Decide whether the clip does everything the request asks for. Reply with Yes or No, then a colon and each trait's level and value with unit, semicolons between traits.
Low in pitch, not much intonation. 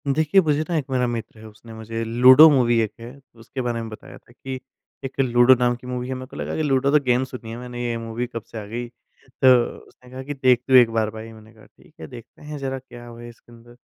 Yes: low, 125 Hz; narrow, 2.3 semitones